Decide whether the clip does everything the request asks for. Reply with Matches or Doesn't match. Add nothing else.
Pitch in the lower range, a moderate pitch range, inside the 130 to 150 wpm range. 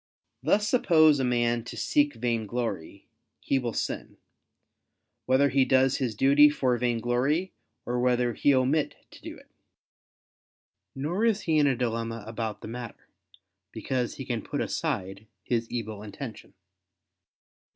Matches